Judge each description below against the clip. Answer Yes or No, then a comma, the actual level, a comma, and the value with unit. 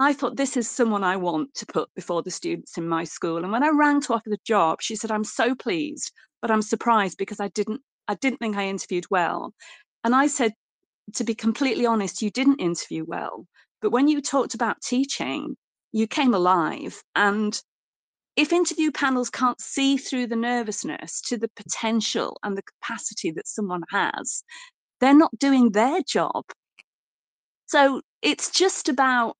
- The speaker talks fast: No, average, 180 wpm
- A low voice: No, high, 230 Hz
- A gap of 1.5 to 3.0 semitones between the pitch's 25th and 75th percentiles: No, average, 4.8 semitones